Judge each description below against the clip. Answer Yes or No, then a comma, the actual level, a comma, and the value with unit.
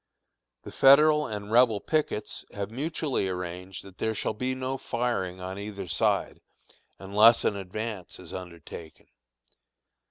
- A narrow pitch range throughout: No, average, 5.1 semitones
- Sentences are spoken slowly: Yes, slow, 130 wpm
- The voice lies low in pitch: Yes, low, 105 Hz